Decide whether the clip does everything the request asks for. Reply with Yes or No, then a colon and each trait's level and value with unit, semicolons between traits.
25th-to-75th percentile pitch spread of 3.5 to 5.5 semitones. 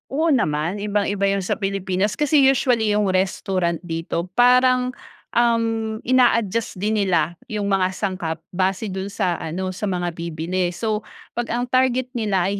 Yes: average, 4.0 semitones